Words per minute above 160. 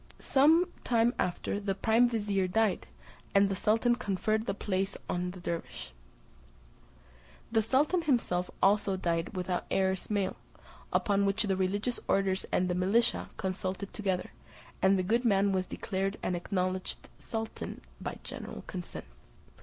No: average, 140 wpm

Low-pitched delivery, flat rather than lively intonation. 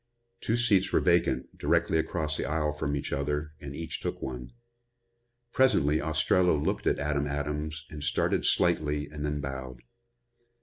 Yes: very low, 75 Hz; narrow, 1.8 semitones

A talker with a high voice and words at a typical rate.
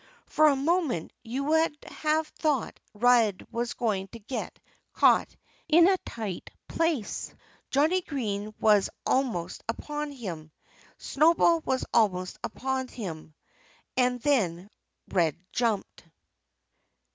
No: high, 245 Hz; slow, 110 wpm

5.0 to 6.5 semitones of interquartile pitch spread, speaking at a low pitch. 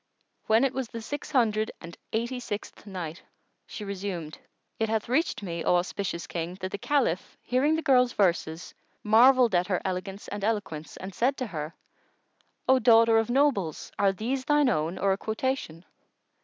No: wide, 5.5 semitones; high, 210 Hz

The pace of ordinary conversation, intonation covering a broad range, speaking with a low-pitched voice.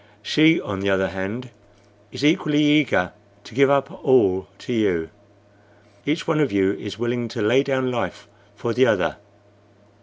Yes: average, 160 wpm; wide, 5.9 semitones; low, 120 Hz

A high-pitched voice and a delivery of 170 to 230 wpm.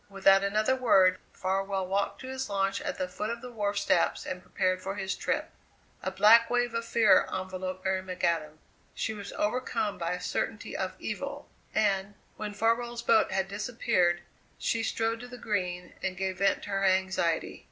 Yes: high, 195 Hz; average, 180 wpm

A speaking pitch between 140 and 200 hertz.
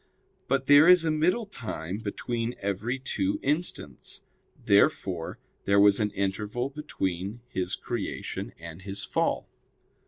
No: low, 105 Hz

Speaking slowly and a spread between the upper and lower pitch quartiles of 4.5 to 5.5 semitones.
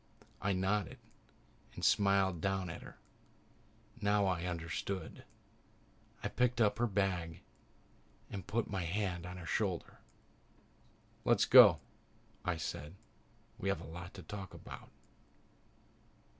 No: slow, 120 wpm; narrow, 2.5 semitones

